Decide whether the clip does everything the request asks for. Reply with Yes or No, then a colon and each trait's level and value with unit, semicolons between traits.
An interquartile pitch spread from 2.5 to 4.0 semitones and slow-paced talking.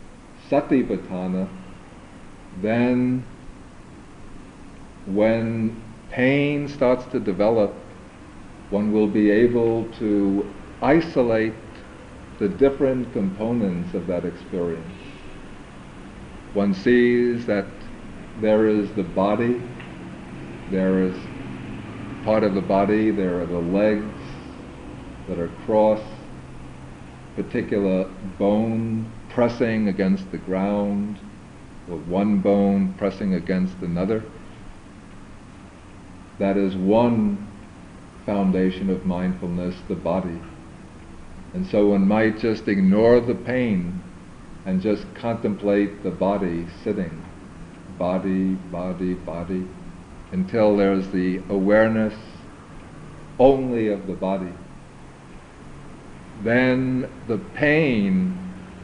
Yes: average, 3.1 semitones; slow, 90 wpm